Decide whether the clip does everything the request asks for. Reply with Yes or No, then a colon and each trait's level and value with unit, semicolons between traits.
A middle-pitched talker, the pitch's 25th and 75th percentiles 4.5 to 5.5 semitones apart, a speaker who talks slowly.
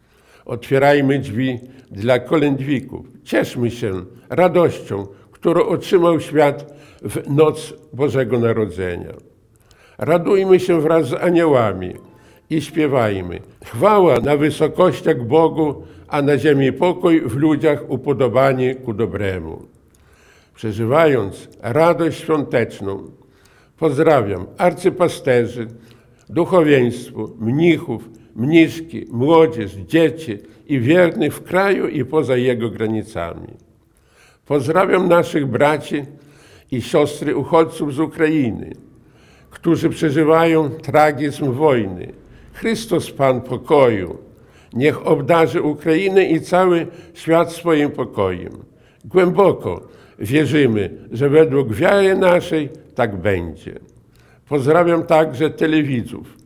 Yes: medium, 145 Hz; average, 5.2 semitones; slow, 90 wpm